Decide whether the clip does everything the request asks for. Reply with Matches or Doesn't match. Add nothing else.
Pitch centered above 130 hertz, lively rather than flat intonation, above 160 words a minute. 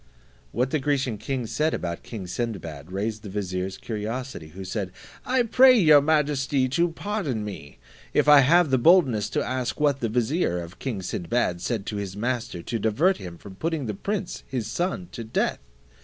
Doesn't match